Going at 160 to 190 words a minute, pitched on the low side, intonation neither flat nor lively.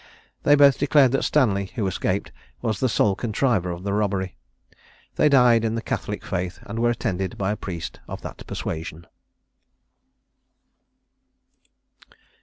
No: average, 140 wpm; low, 105 Hz; average, 4.6 semitones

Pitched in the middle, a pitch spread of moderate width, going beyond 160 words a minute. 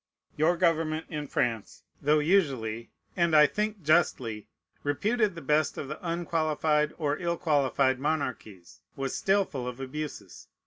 No: medium, 150 Hz; average, 4.0 semitones; average, 140 wpm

